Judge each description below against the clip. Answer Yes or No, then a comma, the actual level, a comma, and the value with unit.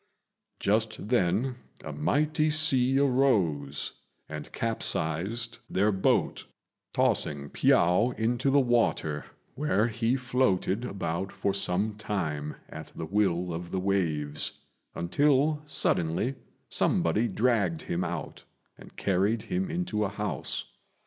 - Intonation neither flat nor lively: No, wide, 6.2 semitones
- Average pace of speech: No, slow, 115 wpm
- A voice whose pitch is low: Yes, low, 105 Hz